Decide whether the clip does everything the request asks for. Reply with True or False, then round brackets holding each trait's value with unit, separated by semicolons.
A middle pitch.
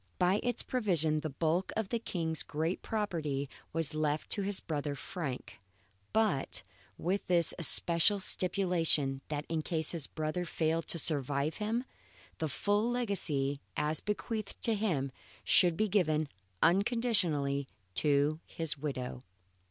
True (165 Hz)